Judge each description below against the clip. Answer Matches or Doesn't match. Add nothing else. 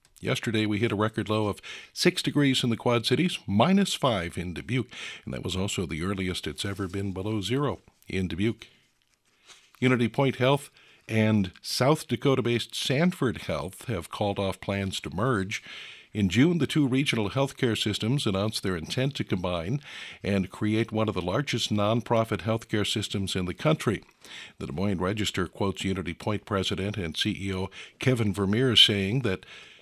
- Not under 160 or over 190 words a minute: Matches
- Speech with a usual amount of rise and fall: Matches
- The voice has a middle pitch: Doesn't match